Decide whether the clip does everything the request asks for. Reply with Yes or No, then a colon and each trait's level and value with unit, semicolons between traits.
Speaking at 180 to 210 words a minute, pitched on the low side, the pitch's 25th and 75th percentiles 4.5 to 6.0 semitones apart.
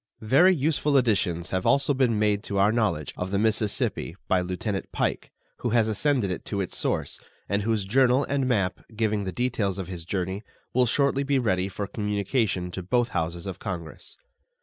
Yes: average, 185 wpm; low, 105 Hz; average, 4.8 semitones